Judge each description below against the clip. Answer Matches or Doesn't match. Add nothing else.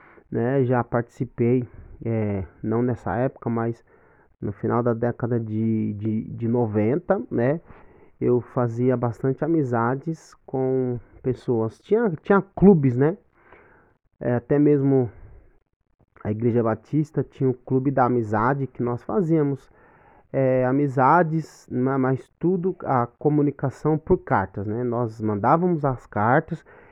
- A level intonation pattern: Doesn't match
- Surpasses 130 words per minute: Doesn't match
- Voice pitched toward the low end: Matches